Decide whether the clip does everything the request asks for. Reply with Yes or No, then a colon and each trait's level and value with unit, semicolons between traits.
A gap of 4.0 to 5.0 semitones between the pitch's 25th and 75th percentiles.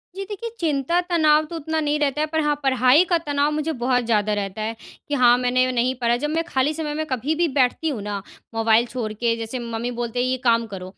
Yes: average, 4.6 semitones